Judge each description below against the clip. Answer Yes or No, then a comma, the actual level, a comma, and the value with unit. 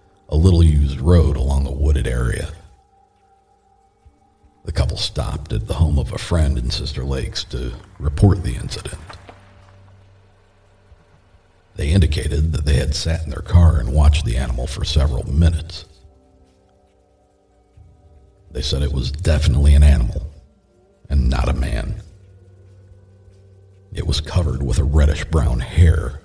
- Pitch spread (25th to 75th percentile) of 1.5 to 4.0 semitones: No, average, 5.2 semitones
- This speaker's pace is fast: No, slow, 135 wpm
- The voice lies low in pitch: Yes, very low, 80 Hz